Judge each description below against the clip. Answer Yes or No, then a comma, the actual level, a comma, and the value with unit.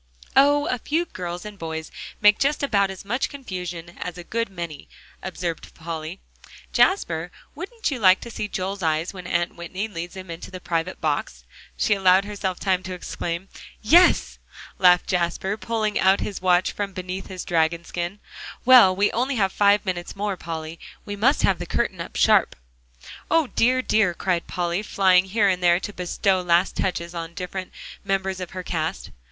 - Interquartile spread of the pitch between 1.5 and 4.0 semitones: Yes, average, 3.1 semitones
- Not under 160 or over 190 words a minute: Yes, average, 180 wpm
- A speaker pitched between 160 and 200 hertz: Yes, medium, 185 Hz